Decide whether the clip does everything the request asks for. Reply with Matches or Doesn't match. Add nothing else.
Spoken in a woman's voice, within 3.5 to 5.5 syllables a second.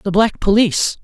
Doesn't match